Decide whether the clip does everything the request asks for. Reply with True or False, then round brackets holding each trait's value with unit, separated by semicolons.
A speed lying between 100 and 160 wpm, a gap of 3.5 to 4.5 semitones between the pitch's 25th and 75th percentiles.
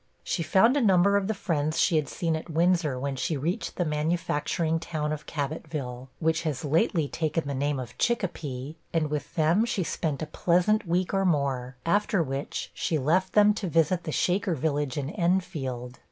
False (185 wpm; 3.8 semitones)